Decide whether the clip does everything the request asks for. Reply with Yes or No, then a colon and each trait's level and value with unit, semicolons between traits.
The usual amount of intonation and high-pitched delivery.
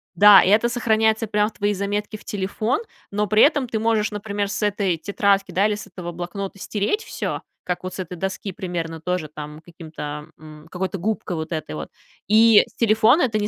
Yes: average, 3.4 semitones; high, 200 Hz